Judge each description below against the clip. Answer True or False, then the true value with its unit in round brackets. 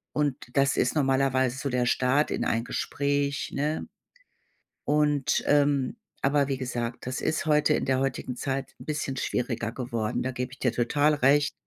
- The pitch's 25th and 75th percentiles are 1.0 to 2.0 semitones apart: False (2.4 semitones)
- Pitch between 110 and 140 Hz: True (135 Hz)